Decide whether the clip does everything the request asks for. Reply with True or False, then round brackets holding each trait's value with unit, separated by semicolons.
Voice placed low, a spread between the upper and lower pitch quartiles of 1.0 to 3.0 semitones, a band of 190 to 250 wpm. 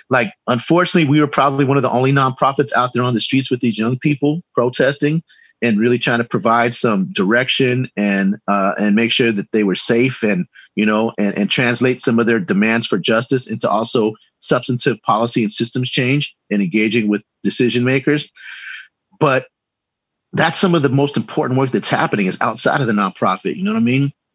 False (125 Hz; 3.8 semitones; 195 wpm)